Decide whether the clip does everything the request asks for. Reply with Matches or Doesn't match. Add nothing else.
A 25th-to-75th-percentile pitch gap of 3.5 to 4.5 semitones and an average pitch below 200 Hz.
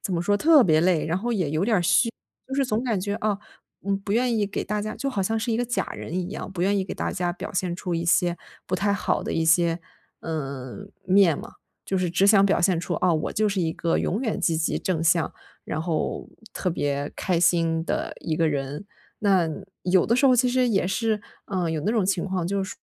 Matches